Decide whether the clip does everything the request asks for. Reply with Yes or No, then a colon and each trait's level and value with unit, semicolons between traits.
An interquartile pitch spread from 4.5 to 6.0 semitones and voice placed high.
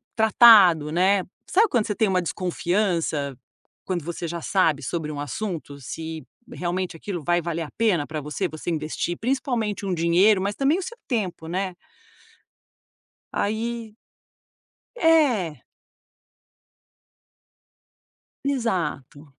No: average, 5.2 semitones; medium, 180 Hz